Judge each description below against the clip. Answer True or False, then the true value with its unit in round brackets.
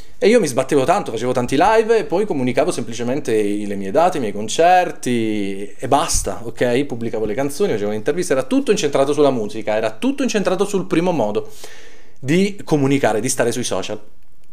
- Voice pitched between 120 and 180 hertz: True (135 Hz)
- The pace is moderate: False (180 wpm)